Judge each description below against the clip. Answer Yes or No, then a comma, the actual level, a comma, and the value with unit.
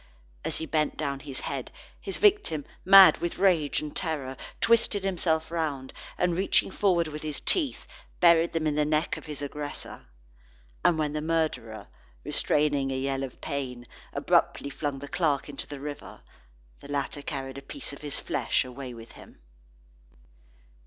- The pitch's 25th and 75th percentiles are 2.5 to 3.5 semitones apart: Yes, average, 3.1 semitones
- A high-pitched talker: No, medium, 150 Hz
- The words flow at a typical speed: Yes, average, 165 wpm